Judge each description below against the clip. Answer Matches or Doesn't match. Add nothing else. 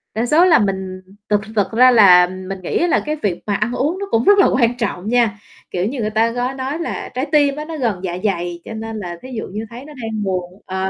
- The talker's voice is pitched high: Matches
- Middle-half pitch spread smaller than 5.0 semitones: Doesn't match